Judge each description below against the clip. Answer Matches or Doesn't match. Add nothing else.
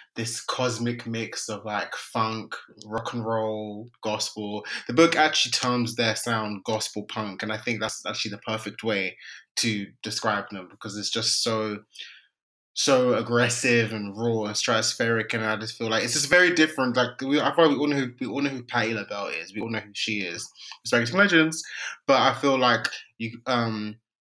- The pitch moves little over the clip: Matches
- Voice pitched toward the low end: Matches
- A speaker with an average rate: Matches